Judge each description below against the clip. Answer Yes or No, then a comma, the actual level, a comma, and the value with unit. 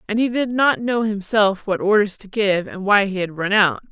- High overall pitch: Yes, high, 205 Hz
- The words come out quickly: Yes, fast, 245 wpm